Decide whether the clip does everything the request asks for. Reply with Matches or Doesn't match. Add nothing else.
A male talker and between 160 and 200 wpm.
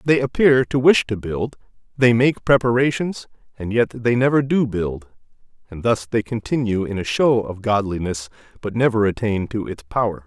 Matches